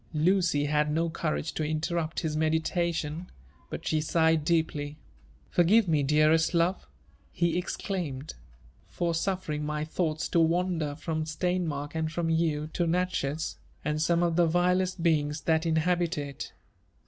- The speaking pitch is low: No, medium, 160 Hz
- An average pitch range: No, narrow, 2.1 semitones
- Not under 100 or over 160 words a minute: Yes, average, 140 wpm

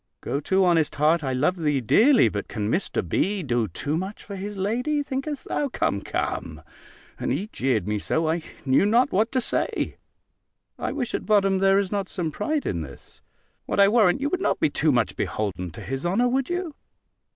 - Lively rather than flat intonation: Yes, wide, 8.7 semitones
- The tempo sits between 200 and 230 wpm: Yes, fast, 205 wpm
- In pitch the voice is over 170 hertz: Yes, high, 190 Hz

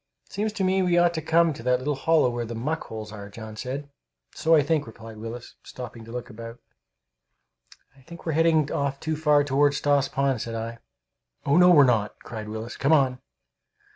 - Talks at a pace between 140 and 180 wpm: No, fast, 205 wpm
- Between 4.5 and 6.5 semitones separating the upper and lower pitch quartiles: Yes, wide, 5.5 semitones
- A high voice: No, low, 135 Hz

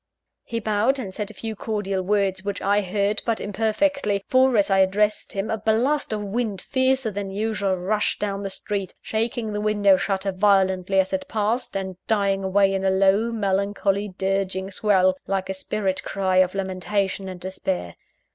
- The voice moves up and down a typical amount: No, narrow, 2.0 semitones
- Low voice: No, high, 200 Hz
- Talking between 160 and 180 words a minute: Yes, average, 175 wpm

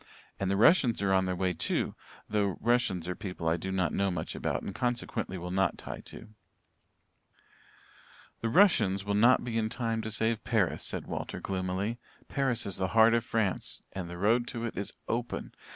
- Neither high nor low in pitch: No, low, 100 Hz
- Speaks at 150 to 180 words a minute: No, average, 190 wpm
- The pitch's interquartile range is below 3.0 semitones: No, average, 3.7 semitones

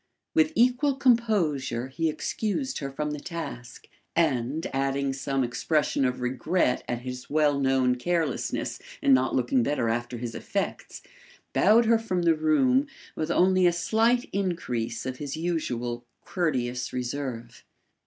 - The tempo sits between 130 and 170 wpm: Yes, average, 140 wpm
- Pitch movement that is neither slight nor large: No, wide, 6.2 semitones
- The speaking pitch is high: No, medium, 145 Hz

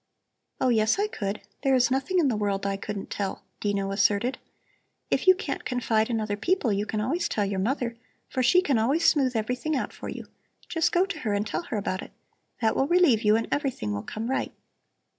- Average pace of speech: No, fast, 215 wpm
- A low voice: No, high, 230 Hz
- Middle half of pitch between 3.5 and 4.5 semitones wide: No, average, 5.1 semitones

